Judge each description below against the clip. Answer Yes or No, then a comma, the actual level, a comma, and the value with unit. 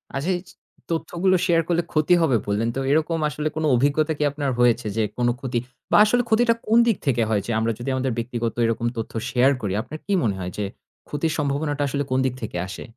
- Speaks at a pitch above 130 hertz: Yes, medium, 140 Hz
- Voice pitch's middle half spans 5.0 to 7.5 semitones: Yes, average, 5.3 semitones